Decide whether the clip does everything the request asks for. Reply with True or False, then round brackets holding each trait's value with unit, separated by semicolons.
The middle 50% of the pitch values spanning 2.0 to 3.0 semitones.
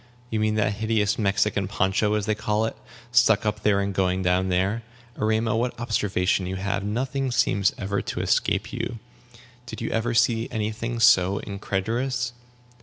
True (2.5 semitones)